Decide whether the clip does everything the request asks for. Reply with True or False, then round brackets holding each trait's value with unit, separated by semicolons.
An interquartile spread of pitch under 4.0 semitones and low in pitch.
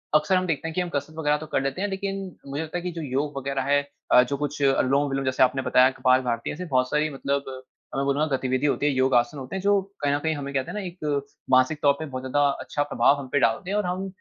False (3.2 semitones; 145 Hz)